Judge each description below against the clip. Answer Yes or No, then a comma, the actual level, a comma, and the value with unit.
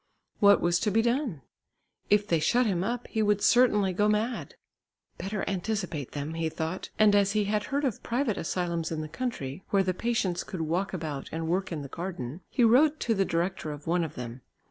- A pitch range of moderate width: Yes, average, 4.9 semitones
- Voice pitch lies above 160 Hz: Yes, high, 190 Hz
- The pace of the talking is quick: Yes, fast, 210 wpm